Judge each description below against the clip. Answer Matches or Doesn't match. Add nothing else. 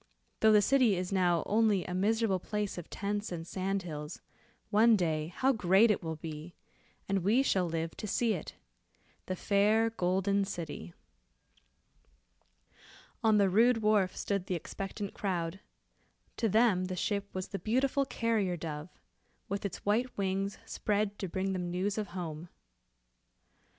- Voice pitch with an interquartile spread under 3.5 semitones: Matches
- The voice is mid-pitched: Doesn't match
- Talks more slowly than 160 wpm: Matches